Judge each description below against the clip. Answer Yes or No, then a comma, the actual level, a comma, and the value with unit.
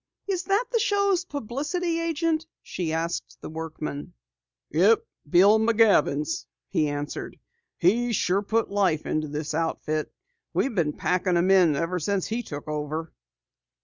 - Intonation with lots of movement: Yes, wide, 7.6 semitones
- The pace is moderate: Yes, average, 145 wpm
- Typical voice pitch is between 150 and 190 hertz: Yes, medium, 185 Hz